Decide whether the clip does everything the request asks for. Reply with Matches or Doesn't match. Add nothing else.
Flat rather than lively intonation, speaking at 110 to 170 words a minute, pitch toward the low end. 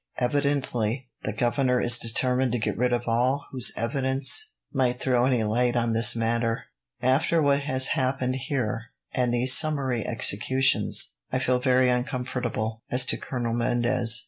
Matches